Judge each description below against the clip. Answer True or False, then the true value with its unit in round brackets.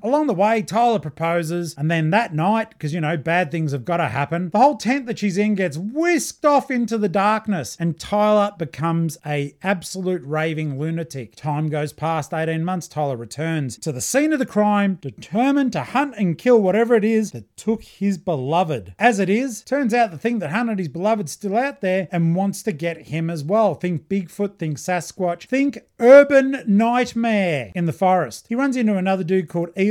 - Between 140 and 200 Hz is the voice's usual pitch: True (190 Hz)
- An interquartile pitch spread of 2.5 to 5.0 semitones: False (5.5 semitones)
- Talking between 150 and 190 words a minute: False (205 wpm)